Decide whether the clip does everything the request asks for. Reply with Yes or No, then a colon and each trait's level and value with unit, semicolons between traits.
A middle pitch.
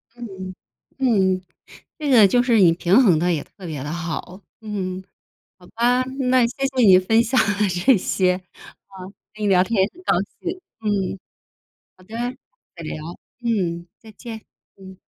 No: high, 195 Hz